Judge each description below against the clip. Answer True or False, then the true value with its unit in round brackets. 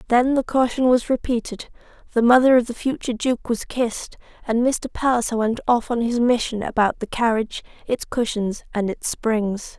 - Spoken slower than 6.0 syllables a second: True (5.1 syllables/s)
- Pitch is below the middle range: False (235 Hz)